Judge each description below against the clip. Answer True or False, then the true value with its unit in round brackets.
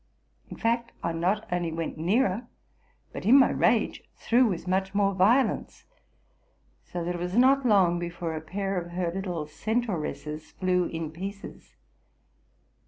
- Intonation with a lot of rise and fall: False (3.8 semitones)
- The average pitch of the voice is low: False (185 Hz)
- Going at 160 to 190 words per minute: False (150 wpm)